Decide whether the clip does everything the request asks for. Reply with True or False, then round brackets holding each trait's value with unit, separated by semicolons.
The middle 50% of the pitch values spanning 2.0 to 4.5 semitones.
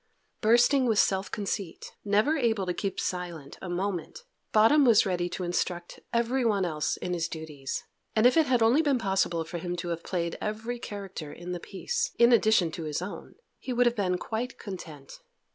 False (5.1 semitones)